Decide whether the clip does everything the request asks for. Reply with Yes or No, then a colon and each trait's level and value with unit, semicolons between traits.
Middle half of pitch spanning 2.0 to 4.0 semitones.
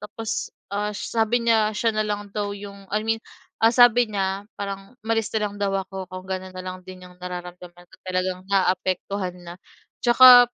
Yes: average, 2.9 semitones